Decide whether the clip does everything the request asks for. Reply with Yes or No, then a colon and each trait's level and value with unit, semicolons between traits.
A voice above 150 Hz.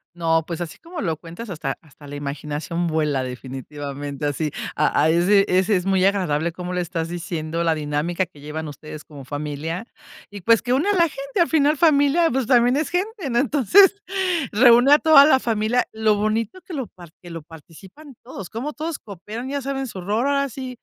Yes: high, 190 Hz